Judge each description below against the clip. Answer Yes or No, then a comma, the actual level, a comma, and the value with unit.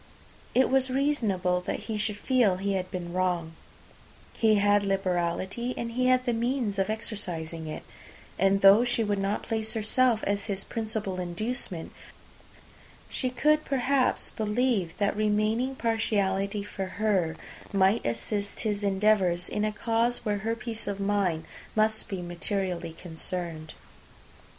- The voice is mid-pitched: No, high, 205 Hz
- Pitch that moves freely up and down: No, average, 3.5 semitones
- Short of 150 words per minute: Yes, average, 140 wpm